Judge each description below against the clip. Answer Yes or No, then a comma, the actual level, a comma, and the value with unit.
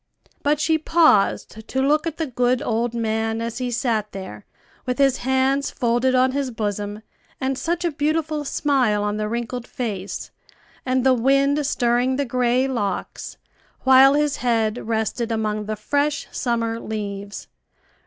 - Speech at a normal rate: Yes, average, 155 wpm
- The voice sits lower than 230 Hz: No, high, 245 Hz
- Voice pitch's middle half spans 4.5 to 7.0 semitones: No, average, 3.8 semitones